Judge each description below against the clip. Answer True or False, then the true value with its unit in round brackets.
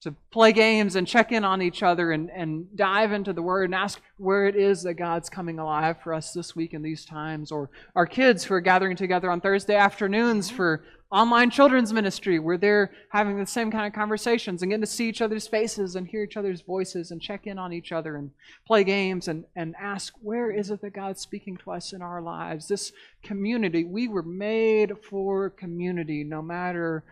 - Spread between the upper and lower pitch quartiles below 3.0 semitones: False (3.4 semitones)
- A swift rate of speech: True (215 wpm)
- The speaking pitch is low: False (190 Hz)